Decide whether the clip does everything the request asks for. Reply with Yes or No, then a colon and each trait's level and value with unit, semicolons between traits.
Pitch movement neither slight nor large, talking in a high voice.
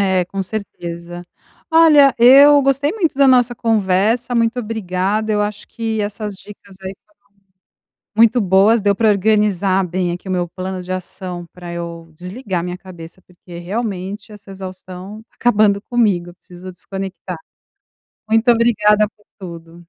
Yes: average, 3.5 semitones; high, 200 Hz